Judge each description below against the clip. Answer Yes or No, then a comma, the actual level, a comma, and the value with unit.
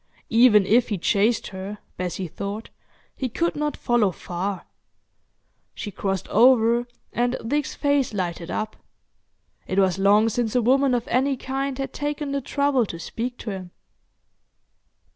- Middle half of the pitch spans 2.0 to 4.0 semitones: No, average, 5.0 semitones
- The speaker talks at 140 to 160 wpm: Yes, average, 145 wpm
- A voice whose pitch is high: Yes, high, 230 Hz